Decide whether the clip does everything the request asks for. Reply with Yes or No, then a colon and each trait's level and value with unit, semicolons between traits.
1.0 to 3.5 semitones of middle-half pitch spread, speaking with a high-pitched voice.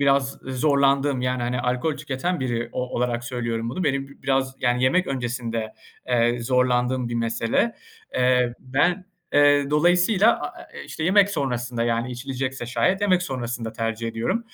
No: average, 3.0 semitones; low, 130 Hz